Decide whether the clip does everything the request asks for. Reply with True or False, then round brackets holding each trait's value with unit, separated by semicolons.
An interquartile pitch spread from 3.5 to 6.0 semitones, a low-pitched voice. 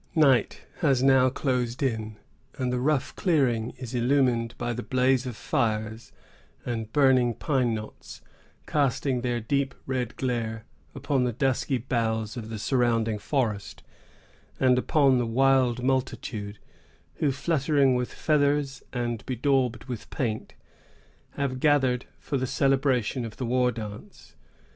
False (2.6 semitones; 125 Hz)